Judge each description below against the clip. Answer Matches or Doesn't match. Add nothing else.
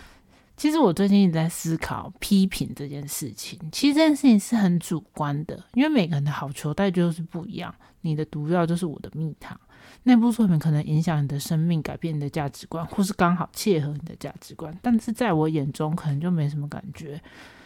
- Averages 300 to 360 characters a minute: Matches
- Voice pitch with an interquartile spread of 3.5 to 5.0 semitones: Matches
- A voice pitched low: Doesn't match